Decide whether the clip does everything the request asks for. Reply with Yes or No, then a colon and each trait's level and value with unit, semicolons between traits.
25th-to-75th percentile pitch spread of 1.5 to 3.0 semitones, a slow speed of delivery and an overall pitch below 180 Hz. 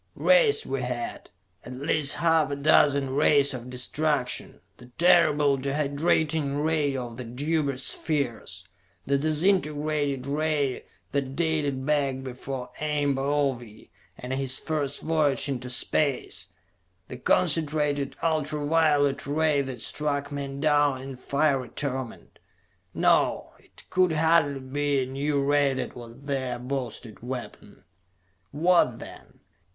Yes: narrow, 2.4 semitones; slow, 125 wpm; medium, 140 Hz